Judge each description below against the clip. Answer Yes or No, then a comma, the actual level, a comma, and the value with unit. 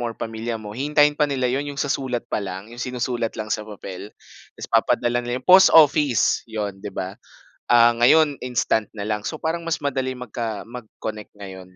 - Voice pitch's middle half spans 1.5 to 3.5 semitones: No, average, 4.4 semitones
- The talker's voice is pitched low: Yes, low, 120 Hz